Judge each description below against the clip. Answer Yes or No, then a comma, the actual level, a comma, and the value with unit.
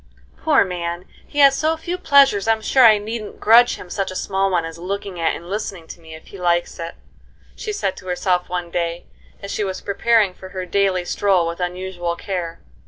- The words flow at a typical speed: No, fast, 210 wpm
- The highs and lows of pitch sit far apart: No, average, 3.5 semitones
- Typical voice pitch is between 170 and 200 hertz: Yes, high, 190 Hz